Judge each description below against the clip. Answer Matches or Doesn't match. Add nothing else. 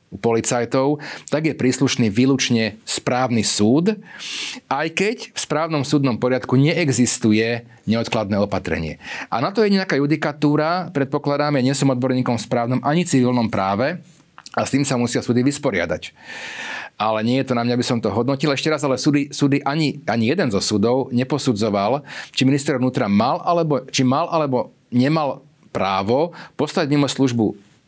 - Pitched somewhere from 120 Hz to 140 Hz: Matches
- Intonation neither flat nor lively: Matches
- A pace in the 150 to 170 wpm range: Matches